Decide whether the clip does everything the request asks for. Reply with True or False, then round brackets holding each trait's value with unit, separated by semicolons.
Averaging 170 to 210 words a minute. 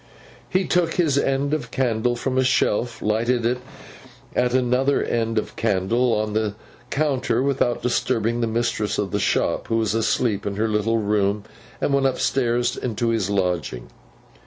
False (160 wpm)